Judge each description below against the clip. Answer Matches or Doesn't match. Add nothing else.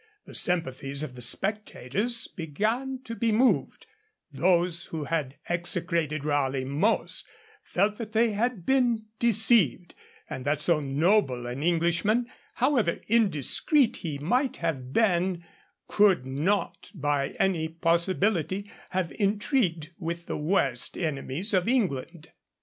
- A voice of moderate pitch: Matches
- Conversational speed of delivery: Doesn't match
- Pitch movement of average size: Doesn't match